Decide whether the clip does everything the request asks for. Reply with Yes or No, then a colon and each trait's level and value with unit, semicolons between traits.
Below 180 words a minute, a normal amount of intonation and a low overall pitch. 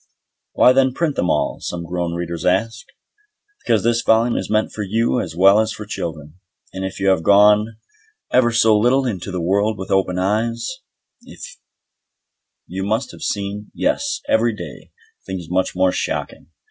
Yes: average, 170 wpm; average, 3.9 semitones; low, 105 Hz